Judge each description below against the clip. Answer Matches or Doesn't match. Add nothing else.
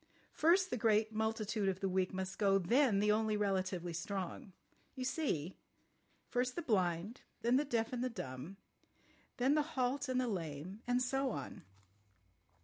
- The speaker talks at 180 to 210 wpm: Doesn't match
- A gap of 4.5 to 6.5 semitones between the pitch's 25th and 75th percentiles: Matches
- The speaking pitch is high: Matches